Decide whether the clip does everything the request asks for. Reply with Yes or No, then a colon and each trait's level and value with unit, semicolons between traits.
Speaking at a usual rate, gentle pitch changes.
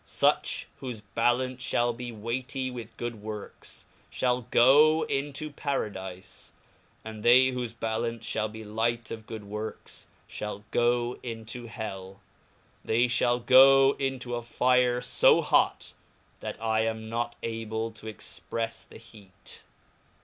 No: slow, 130 wpm; narrow, 2.1 semitones